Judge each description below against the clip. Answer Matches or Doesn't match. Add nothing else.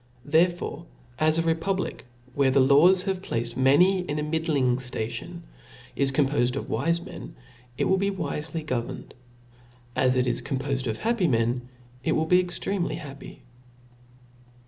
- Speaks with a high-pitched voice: Doesn't match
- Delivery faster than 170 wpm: Doesn't match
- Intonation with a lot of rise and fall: Doesn't match